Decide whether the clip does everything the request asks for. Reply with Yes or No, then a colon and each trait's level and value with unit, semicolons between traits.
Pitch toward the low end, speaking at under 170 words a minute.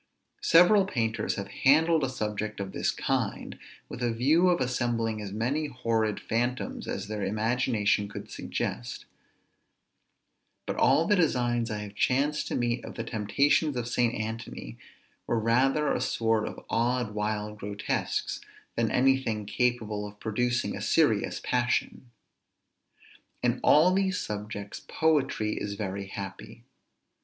Yes: low, 115 Hz; average, 140 wpm